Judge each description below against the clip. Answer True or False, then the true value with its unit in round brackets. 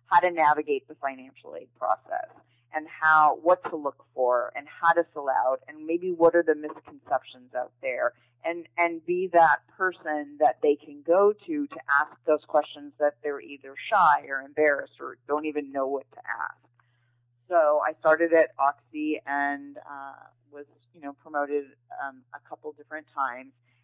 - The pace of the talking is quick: False (175 wpm)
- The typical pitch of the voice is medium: True (150 Hz)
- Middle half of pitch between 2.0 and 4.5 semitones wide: True (3.1 semitones)